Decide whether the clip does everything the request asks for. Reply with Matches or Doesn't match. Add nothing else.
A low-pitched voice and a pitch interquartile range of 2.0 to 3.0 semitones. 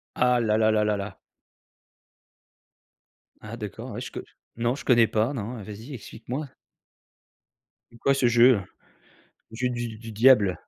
Matches